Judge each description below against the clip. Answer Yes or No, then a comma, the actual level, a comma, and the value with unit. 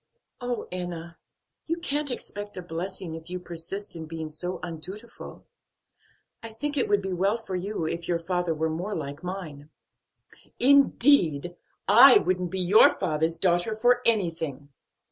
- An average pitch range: Yes, average, 4.2 semitones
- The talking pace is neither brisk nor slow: Yes, average, 150 wpm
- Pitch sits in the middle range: Yes, medium, 180 Hz